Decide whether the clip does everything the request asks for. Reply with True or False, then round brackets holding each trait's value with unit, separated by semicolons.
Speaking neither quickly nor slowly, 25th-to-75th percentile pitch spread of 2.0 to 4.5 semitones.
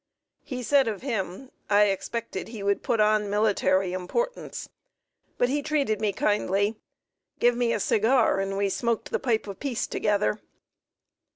True (155 wpm; 3.4 semitones)